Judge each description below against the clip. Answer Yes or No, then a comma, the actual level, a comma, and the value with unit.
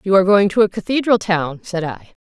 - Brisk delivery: Yes, fast, 240 wpm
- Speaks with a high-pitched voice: Yes, high, 195 Hz